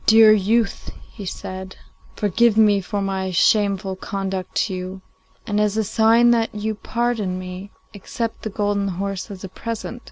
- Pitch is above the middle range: Yes, high, 205 Hz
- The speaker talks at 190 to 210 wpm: No, average, 160 wpm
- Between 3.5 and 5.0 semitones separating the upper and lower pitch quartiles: No, narrow, 2.6 semitones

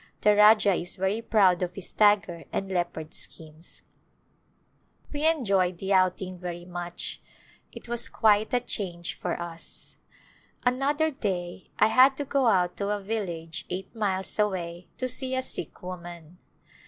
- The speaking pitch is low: No, high, 190 Hz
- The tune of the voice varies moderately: Yes, average, 4.0 semitones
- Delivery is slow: No, average, 155 wpm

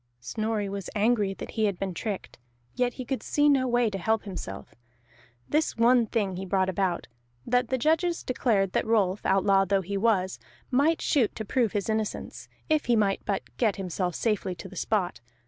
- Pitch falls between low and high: No, high, 210 Hz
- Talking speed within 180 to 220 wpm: Yes, average, 190 wpm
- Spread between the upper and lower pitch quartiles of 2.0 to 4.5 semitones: Yes, average, 4.0 semitones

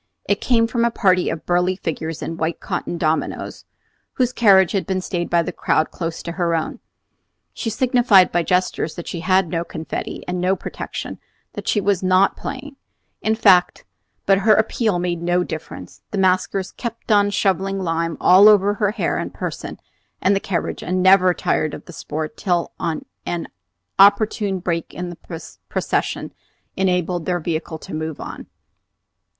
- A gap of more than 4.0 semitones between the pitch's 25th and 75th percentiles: No, average, 2.9 semitones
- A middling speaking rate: Yes, average, 170 wpm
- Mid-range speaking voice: Yes, medium, 180 Hz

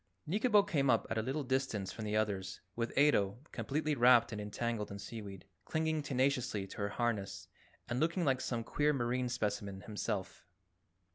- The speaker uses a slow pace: No, average, 165 wpm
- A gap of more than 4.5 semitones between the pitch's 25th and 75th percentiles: Yes, average, 5.1 semitones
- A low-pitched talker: Yes, low, 120 Hz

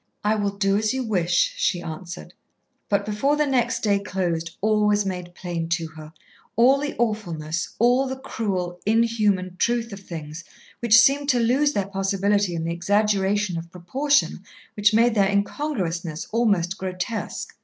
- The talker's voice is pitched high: Yes, high, 205 Hz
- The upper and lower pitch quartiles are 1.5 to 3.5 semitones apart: No, average, 4.7 semitones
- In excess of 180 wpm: No, average, 160 wpm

